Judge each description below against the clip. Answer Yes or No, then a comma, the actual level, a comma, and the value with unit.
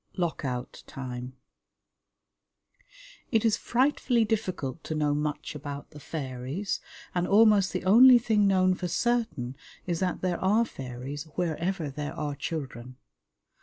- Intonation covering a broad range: Yes, wide, 6.2 semitones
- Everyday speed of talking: No, slow, 130 wpm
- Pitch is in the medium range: Yes, medium, 170 Hz